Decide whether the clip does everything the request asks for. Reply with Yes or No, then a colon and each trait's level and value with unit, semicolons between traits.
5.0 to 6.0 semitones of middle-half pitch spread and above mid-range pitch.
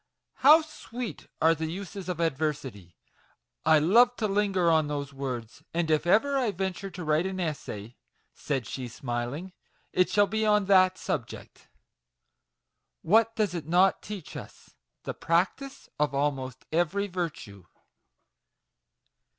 No: wide, 5.4 semitones; medium, 175 Hz